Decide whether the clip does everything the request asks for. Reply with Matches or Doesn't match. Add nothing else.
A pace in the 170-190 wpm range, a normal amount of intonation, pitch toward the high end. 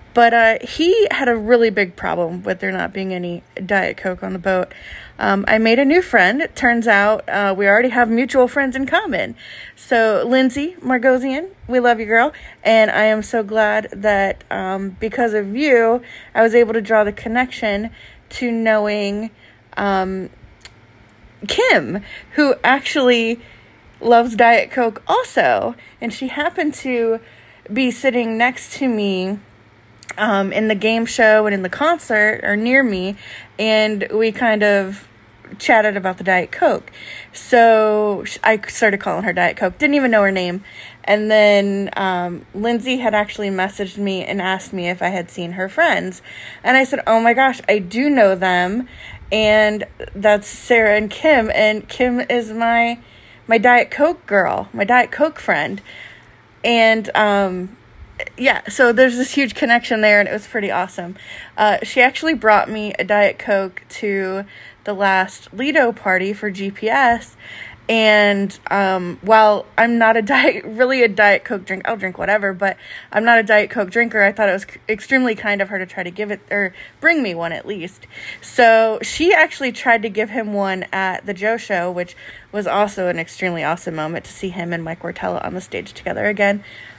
Matches